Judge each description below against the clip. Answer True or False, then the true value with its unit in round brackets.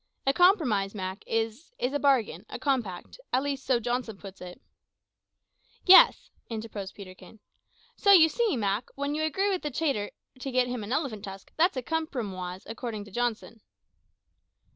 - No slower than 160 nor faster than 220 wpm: True (165 wpm)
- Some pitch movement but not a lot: False (6.2 semitones)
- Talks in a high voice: True (245 Hz)